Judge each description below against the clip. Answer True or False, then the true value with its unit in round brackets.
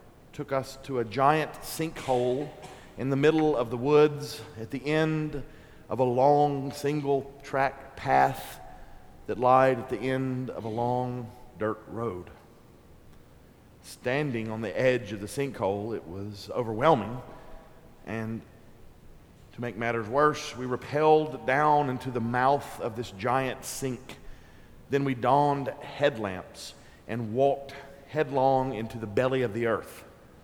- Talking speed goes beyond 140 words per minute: False (135 wpm)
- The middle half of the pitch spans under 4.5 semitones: True (3.9 semitones)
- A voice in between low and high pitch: False (130 Hz)